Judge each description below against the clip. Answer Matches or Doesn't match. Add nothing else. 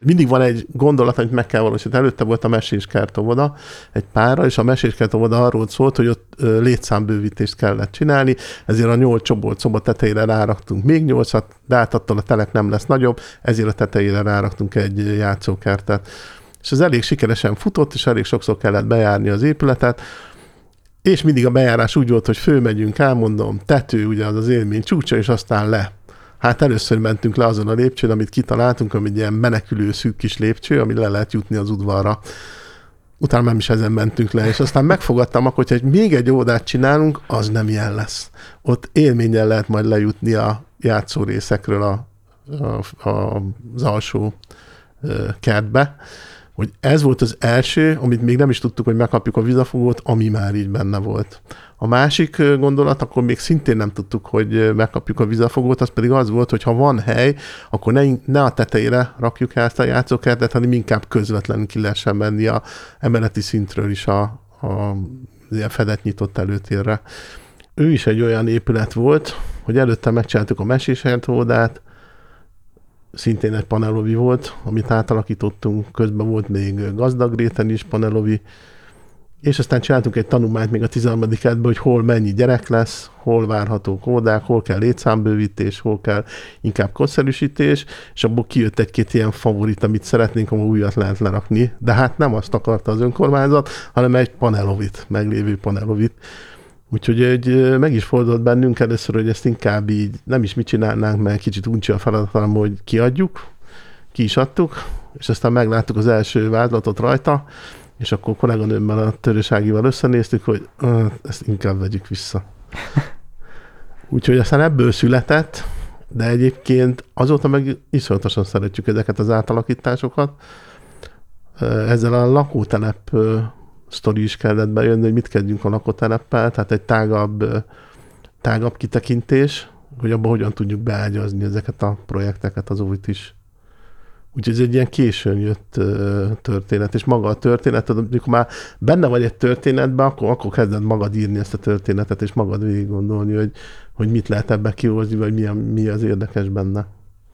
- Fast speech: Matches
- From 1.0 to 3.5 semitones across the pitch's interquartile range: Matches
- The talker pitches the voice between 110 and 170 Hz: Matches